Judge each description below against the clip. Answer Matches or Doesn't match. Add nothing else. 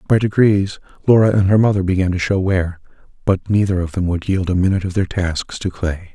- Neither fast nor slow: Doesn't match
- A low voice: Matches